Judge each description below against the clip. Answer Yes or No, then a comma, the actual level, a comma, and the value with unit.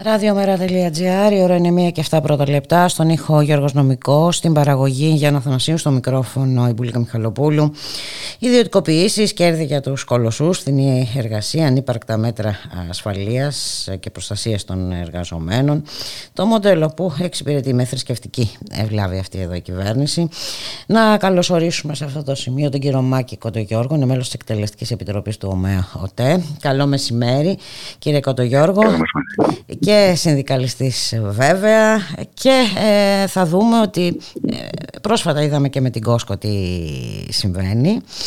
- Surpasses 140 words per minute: No, average, 135 wpm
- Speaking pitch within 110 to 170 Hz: Yes, medium, 140 Hz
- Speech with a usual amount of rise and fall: No, wide, 6.7 semitones